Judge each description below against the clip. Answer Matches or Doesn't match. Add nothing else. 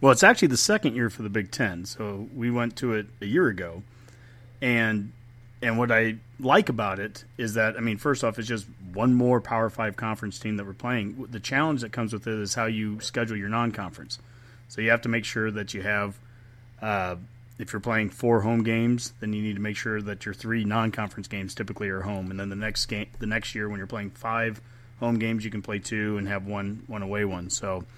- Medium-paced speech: Doesn't match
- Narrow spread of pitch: Matches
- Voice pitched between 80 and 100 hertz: Doesn't match